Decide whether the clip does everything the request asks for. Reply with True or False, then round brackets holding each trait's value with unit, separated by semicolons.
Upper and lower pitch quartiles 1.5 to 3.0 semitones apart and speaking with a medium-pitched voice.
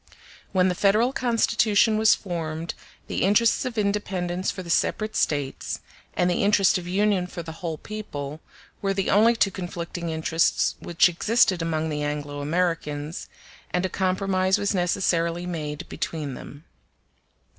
False (3.7 semitones; 180 Hz)